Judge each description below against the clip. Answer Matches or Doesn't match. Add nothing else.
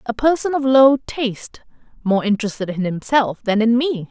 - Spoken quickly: Doesn't match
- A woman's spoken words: Matches